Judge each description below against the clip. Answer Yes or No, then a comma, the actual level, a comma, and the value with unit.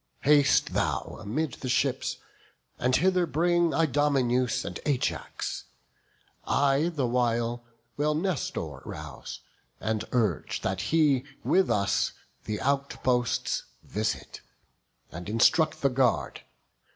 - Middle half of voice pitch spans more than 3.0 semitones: Yes, average, 4.5 semitones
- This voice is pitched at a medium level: No, low, 130 Hz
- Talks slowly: Yes, slow, 105 wpm